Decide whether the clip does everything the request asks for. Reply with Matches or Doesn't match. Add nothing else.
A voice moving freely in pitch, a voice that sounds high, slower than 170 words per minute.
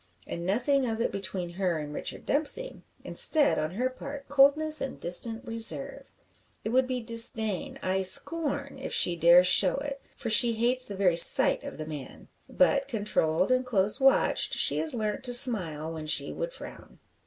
Doesn't match